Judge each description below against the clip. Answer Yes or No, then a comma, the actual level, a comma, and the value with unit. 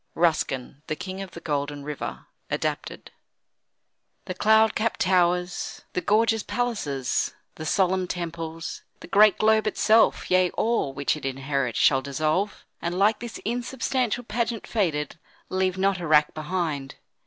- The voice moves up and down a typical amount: No, wide, 6.1 semitones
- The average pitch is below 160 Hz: No, medium, 180 Hz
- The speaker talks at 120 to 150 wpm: Yes, average, 140 wpm